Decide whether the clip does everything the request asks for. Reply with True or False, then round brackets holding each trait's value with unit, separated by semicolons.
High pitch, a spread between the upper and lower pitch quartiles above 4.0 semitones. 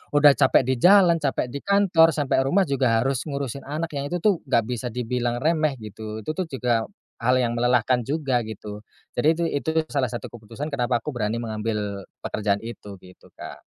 False (125 Hz; 4.4 semitones)